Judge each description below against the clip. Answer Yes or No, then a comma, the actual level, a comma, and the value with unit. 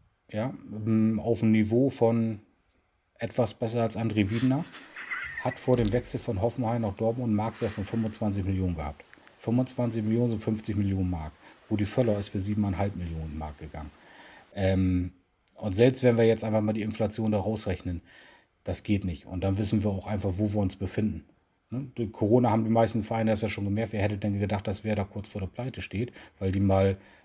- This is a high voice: No, low, 105 Hz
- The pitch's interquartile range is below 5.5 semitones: Yes, average, 2.8 semitones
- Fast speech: Yes, fast, 200 wpm